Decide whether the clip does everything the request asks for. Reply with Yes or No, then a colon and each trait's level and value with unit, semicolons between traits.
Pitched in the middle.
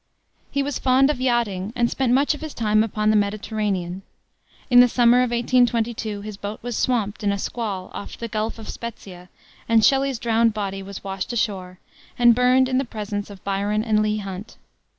No: high, 220 Hz